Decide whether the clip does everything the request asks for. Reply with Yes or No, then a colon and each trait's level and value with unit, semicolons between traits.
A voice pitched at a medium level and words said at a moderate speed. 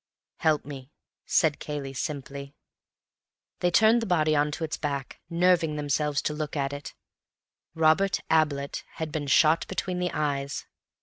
Yes: medium, 150 Hz; average, 145 wpm